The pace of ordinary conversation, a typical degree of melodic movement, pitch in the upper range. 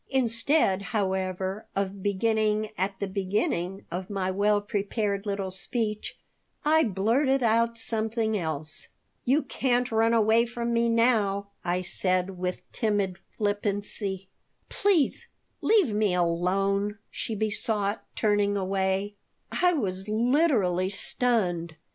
No: slow, 115 wpm; average, 3.2 semitones; high, 205 Hz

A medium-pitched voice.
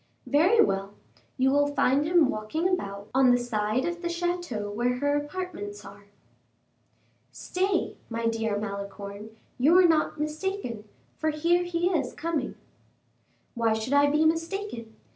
No: very high, 285 Hz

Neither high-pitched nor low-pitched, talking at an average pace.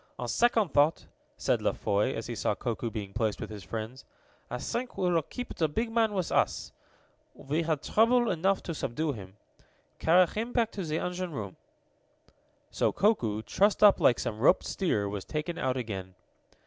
Yes: medium, 155 Hz; average, 185 wpm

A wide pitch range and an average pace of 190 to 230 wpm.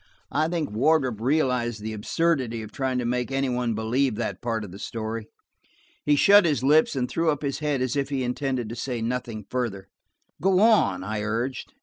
No: average, 4.2 semitones; average, 200 wpm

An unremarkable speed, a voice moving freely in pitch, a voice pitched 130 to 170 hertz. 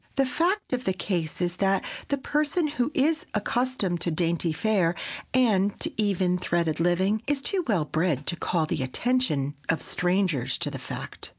No: average, 175 wpm; wide, 7.2 semitones; high, 190 Hz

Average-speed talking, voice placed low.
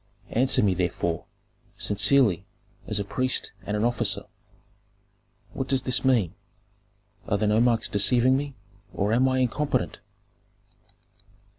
No: slow, 120 wpm; low, 115 Hz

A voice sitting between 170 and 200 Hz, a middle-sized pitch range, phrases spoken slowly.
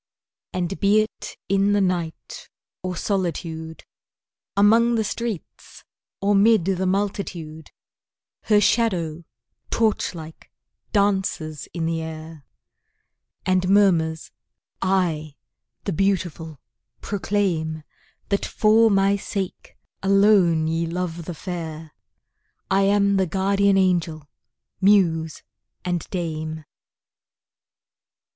Yes: medium, 185 Hz; average, 3.6 semitones; slow, 95 wpm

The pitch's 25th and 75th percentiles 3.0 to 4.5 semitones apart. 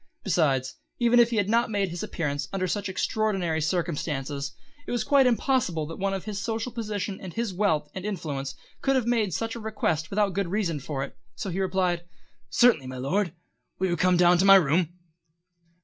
No: average, 5.0 semitones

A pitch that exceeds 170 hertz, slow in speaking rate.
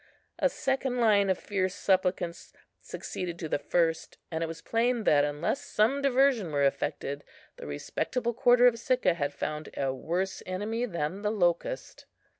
No: high, 190 Hz; average, 160 wpm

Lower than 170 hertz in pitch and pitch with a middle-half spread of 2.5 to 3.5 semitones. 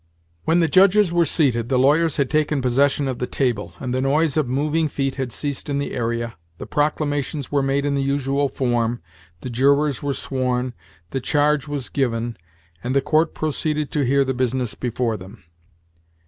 Yes: medium, 140 Hz; average, 2.8 semitones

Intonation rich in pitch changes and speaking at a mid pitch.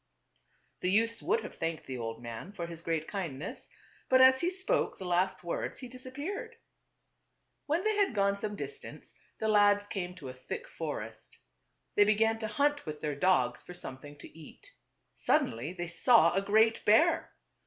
No: wide, 7.7 semitones; high, 205 Hz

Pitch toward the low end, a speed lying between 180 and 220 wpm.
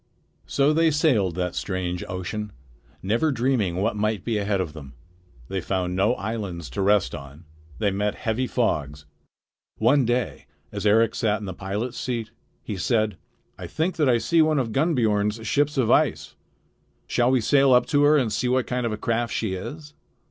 Yes: low, 110 Hz; average, 185 wpm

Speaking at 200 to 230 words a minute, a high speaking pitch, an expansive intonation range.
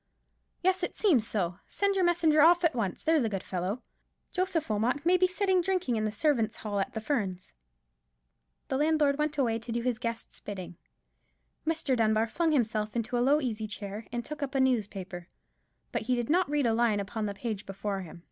Yes: fast, 205 wpm; high, 240 Hz; wide, 6.3 semitones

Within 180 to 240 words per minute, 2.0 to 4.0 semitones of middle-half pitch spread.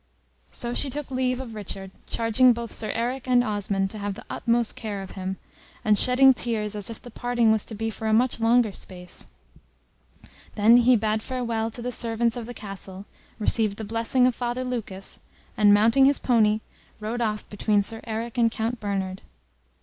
Yes: average, 190 wpm; narrow, 2.6 semitones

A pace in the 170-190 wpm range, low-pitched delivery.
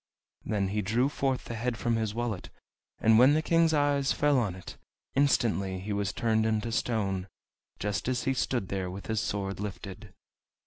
Yes: average, 180 wpm; low, 110 Hz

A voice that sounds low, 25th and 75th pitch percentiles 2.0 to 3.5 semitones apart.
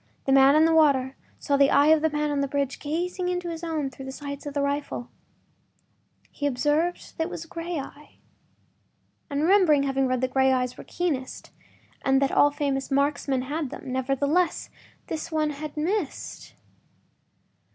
No: very high, 285 Hz; average, 2.7 semitones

